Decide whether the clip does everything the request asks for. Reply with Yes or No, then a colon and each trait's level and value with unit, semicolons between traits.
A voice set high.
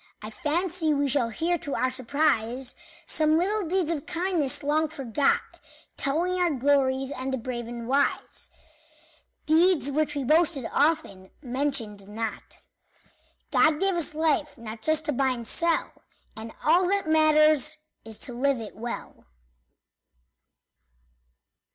Yes: very high, 285 Hz